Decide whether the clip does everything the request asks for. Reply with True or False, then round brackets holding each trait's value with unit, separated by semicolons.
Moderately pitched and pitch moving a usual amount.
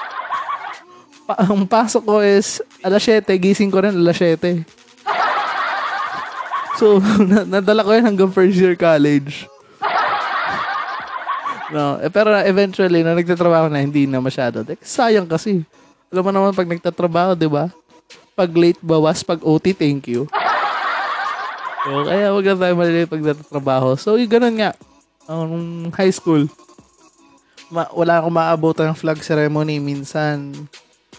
True (175 Hz; 4.2 semitones)